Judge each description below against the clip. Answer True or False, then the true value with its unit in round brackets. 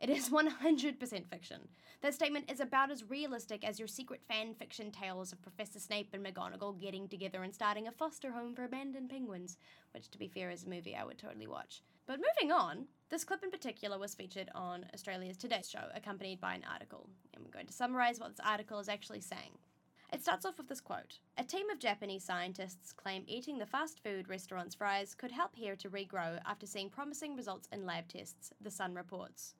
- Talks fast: True (210 wpm)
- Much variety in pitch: True (5.7 semitones)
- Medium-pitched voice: False (210 Hz)